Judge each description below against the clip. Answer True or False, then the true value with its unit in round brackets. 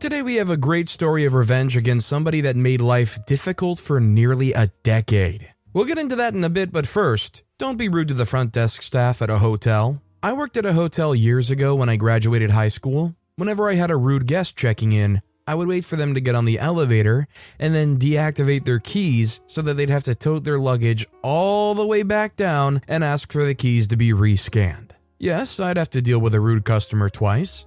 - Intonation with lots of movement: True (6.2 semitones)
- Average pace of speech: False (230 wpm)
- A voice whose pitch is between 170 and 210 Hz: False (135 Hz)